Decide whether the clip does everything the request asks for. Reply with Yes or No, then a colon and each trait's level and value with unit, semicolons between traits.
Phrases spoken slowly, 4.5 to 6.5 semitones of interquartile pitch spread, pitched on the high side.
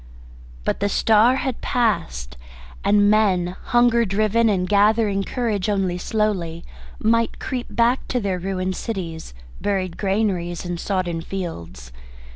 No: slow, 125 wpm; average, 3.6 semitones; high, 200 Hz